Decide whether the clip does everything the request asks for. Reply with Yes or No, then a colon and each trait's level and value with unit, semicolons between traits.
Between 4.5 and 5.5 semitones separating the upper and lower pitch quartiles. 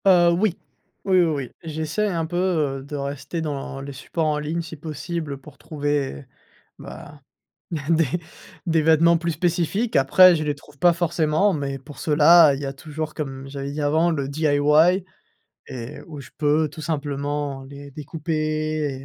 No: average, 2.7 semitones